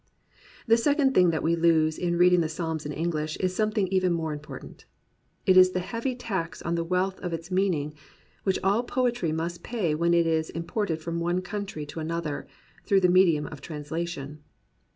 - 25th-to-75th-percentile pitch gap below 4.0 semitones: Yes, average, 2.9 semitones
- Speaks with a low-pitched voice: No, medium, 170 Hz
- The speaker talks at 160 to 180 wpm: No, average, 195 wpm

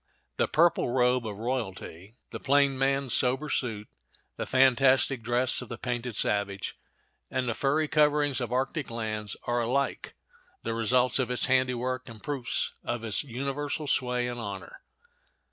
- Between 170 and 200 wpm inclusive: No, average, 150 wpm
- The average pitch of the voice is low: Yes, low, 125 Hz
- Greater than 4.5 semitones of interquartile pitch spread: No, average, 2.7 semitones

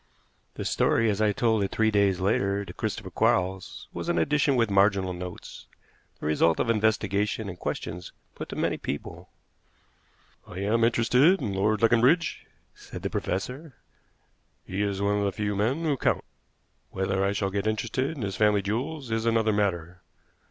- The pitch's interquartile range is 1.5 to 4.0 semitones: Yes, average, 2.9 semitones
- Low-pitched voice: Yes, low, 105 Hz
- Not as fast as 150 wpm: No, average, 170 wpm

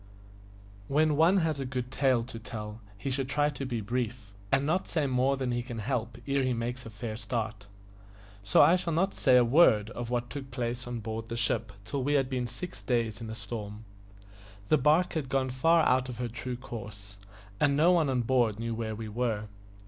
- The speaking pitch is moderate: No, low, 125 Hz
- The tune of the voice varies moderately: Yes, average, 3.3 semitones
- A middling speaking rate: No, fast, 215 wpm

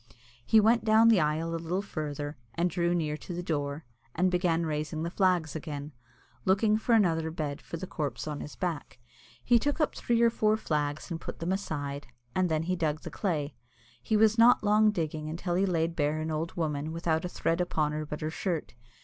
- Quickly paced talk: Yes, fast, 210 wpm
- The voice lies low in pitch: No, medium, 165 Hz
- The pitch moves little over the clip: No, average, 3.6 semitones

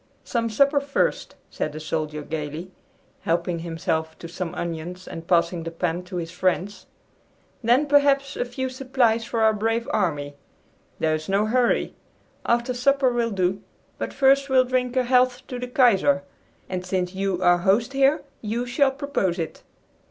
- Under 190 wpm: Yes, average, 165 wpm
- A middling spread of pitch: No, wide, 6.6 semitones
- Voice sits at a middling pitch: No, high, 210 Hz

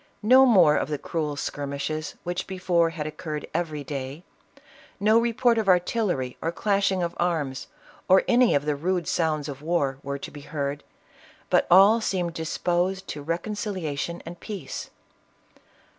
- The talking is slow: No, average, 150 wpm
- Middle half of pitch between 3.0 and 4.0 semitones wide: No, average, 4.4 semitones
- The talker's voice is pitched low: No, medium, 170 Hz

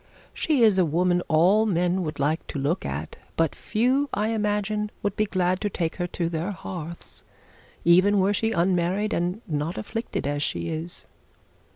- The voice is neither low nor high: Yes, medium, 180 Hz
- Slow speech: No, average, 175 wpm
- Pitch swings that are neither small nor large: Yes, average, 3.9 semitones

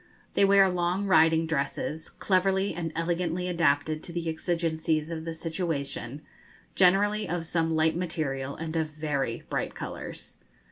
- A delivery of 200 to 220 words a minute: No, average, 140 wpm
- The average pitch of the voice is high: No, medium, 165 Hz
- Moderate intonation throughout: No, narrow, 2.2 semitones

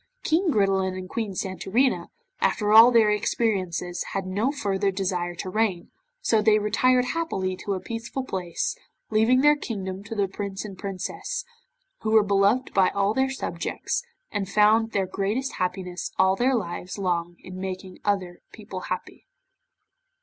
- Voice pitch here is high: Yes, high, 200 Hz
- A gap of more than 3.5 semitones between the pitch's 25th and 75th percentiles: No, average, 3.2 semitones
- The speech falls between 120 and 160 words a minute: Yes, average, 155 wpm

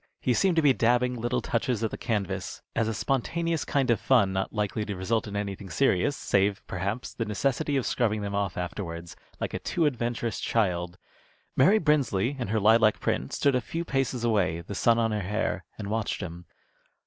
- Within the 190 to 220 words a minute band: Yes, average, 195 wpm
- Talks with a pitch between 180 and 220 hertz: No, low, 110 Hz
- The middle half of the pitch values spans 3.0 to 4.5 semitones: Yes, average, 4.1 semitones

